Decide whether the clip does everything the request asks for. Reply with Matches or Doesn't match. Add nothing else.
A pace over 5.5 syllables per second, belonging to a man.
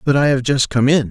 Matches